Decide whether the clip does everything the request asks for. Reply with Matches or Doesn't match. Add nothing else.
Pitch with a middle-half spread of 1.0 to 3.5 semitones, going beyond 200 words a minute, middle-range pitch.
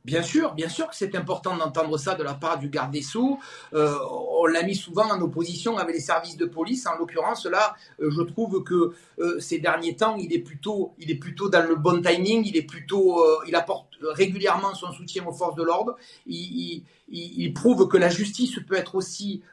Matches